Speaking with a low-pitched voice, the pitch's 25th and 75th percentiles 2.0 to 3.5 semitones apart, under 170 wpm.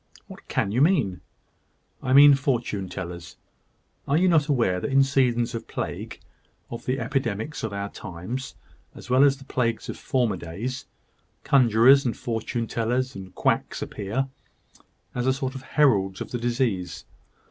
No: low, 120 Hz; average, 4.8 semitones; average, 160 wpm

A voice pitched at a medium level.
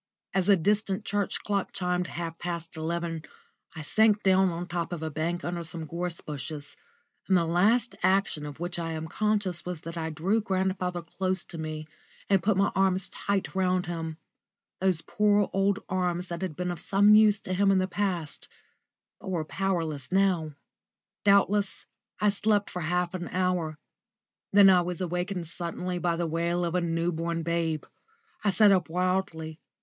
Yes: medium, 180 Hz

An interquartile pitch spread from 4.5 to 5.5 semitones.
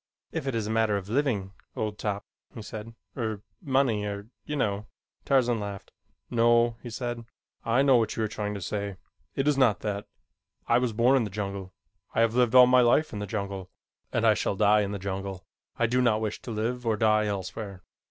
No: average, 3.0 semitones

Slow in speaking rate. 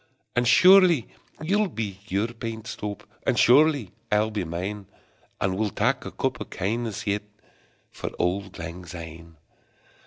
No: average, 145 wpm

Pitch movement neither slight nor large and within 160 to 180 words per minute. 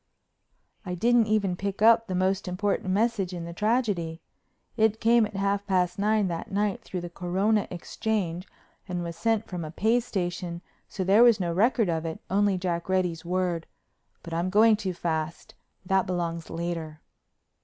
Yes: average, 3.5 semitones; average, 165 wpm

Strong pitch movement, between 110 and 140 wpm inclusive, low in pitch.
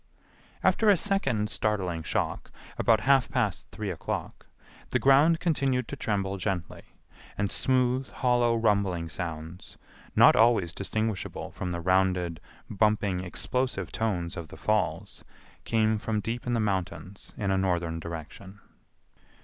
No: average, 4.7 semitones; slow, 135 wpm; low, 100 Hz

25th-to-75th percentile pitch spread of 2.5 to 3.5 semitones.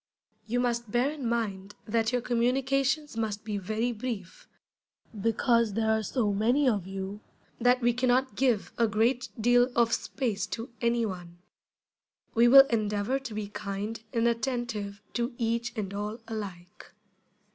Yes: average, 2.8 semitones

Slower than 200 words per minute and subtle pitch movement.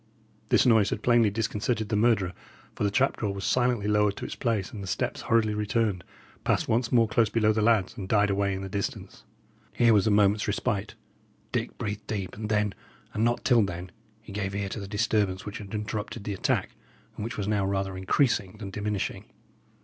No: fast, 205 wpm; narrow, 2.1 semitones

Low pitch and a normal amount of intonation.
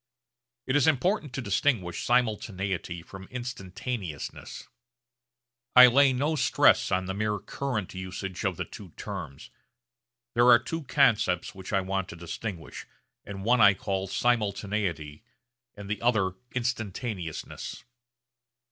Yes: low, 105 Hz; average, 4.8 semitones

